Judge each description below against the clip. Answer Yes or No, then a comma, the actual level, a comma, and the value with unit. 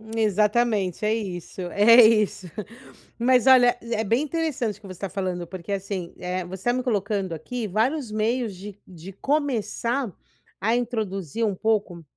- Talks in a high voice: Yes, high, 215 Hz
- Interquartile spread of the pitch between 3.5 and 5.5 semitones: Yes, average, 4.0 semitones